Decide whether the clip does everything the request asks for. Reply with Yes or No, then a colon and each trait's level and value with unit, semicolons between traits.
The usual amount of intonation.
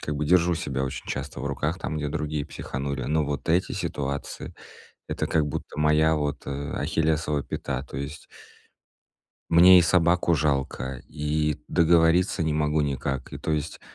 No: narrow, 2.3 semitones